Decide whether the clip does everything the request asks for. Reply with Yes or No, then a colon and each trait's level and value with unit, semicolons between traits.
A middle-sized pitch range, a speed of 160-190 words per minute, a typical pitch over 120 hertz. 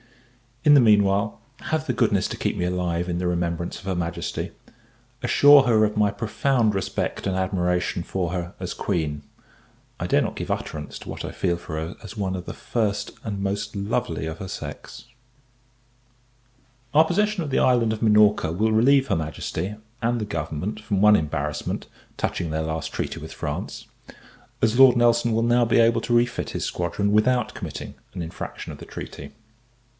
No: average, 5.0 semitones; average, 180 wpm; low, 100 Hz